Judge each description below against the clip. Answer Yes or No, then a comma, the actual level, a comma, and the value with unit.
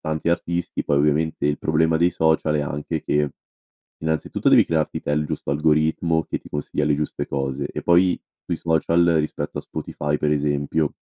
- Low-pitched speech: Yes, very low, 75 Hz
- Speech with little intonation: Yes, narrow, 1.7 semitones